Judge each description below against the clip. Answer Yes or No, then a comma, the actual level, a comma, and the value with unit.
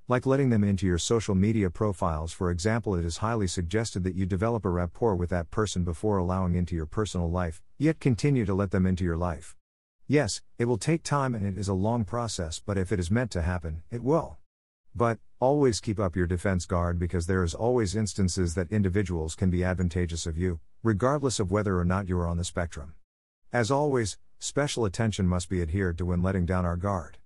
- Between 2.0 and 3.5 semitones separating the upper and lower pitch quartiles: No, average, 4.1 semitones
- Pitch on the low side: Yes, very low, 95 Hz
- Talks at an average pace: No, fast, 215 wpm